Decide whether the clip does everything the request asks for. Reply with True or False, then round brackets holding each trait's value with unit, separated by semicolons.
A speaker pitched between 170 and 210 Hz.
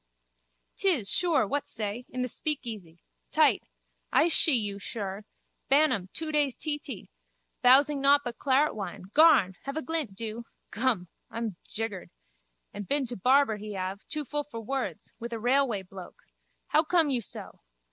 False (245 Hz)